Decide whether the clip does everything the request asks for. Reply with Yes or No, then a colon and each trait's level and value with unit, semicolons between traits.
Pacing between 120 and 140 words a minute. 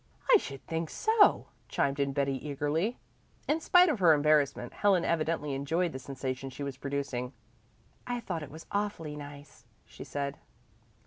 No: average, 155 wpm